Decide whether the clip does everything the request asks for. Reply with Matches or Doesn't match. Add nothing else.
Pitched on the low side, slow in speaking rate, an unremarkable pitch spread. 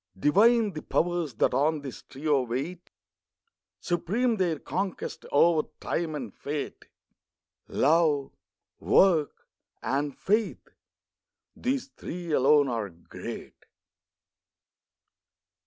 Doesn't match